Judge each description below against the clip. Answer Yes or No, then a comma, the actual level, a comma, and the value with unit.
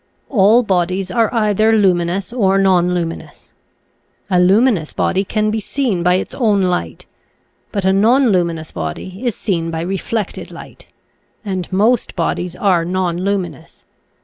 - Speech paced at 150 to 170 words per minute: No, average, 140 wpm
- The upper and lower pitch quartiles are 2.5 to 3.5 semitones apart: Yes, average, 3.2 semitones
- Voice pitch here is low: No, high, 190 Hz